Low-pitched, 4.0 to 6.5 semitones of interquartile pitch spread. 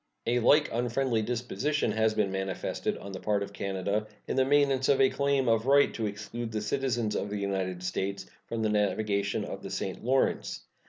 Yes: low, 110 Hz; average, 4.6 semitones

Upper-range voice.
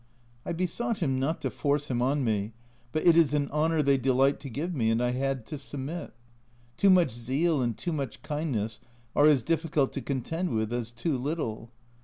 No: medium, 140 Hz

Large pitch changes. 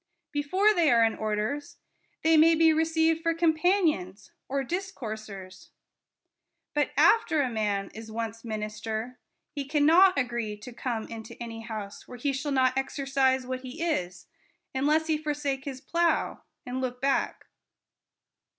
Yes: wide, 5.9 semitones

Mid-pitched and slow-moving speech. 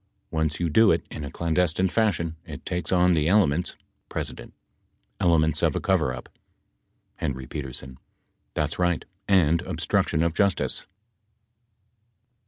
No: very low, 85 Hz; slow, 125 wpm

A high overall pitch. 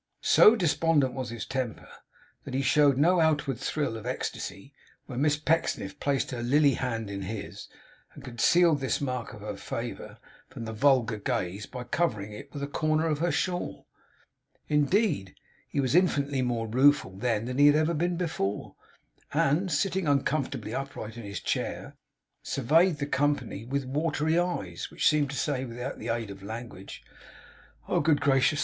No: low, 135 Hz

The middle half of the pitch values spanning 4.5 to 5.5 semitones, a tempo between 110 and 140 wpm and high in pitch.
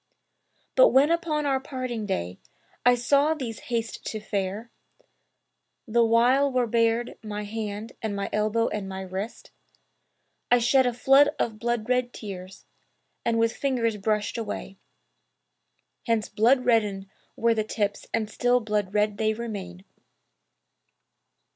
No: average, 2.8 semitones; slow, 135 wpm; high, 225 Hz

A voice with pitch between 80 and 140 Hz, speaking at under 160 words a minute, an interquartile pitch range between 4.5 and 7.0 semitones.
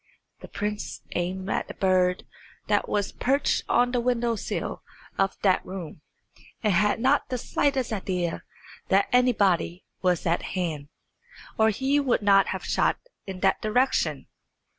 No: high, 205 Hz; average, 145 wpm; average, 5.1 semitones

